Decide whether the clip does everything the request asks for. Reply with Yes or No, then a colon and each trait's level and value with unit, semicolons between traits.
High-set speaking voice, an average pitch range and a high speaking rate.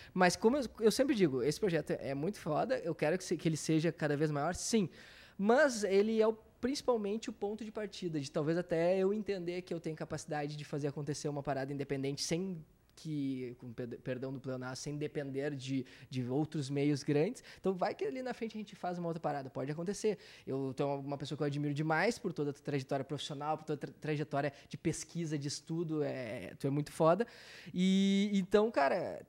No: medium, 160 Hz; average, 4.9 semitones; fast, 210 wpm